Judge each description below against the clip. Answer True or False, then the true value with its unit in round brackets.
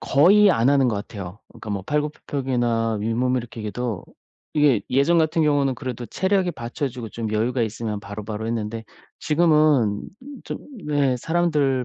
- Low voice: True (125 Hz)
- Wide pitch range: False (4.8 semitones)